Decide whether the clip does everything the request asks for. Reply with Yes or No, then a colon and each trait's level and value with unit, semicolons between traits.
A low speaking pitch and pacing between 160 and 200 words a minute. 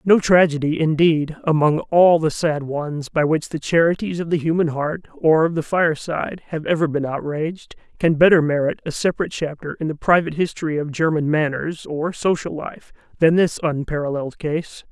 No: medium, 160 Hz; average, 175 wpm